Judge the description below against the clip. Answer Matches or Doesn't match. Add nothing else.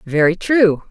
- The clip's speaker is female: Matches